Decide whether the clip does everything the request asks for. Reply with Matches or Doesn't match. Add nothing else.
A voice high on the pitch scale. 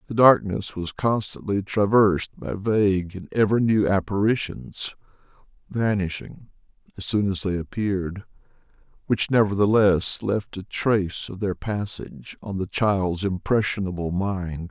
Doesn't match